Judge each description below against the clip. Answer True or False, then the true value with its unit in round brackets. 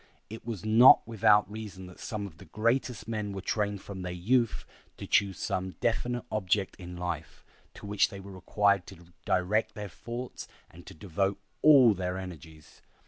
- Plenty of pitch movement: False (3.2 semitones)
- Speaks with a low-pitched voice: True (100 Hz)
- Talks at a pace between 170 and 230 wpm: True (180 wpm)